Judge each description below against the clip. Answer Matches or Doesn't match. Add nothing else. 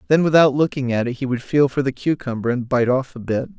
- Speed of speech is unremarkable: Doesn't match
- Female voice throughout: Doesn't match